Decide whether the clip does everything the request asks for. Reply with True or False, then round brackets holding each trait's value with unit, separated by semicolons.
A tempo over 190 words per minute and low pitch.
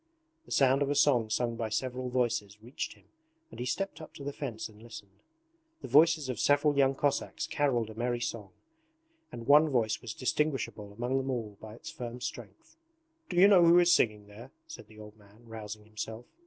True (200 wpm; 120 Hz)